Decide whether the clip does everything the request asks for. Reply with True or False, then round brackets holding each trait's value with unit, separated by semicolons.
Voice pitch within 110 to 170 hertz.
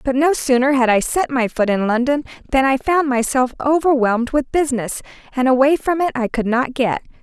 False (260 Hz)